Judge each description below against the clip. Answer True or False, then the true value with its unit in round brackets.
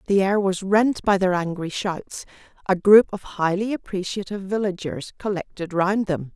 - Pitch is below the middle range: False (190 Hz)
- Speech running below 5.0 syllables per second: True (4.8 syllables/s)